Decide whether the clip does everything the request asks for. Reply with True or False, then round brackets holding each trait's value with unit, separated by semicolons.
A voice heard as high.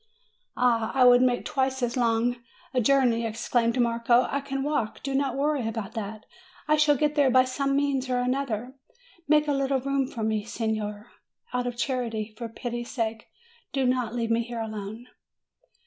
True (245 Hz)